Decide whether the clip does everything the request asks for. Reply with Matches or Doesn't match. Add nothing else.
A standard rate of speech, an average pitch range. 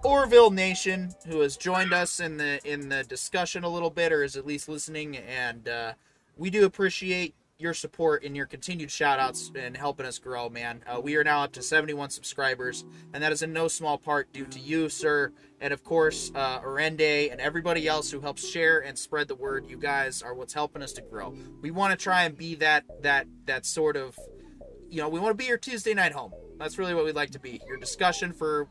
Doesn't match